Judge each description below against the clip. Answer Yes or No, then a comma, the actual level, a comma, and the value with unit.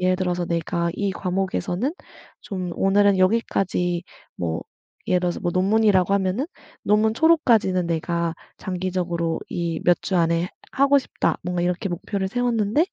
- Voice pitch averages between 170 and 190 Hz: Yes, medium, 185 Hz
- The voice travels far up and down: No, average, 2.8 semitones